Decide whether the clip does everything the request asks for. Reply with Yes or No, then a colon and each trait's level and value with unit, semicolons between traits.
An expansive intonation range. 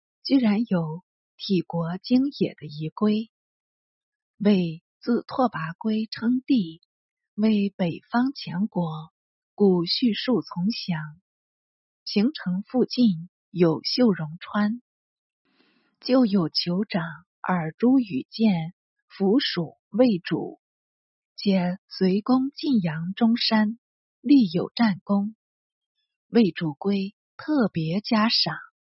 Yes: wide, 5.7 semitones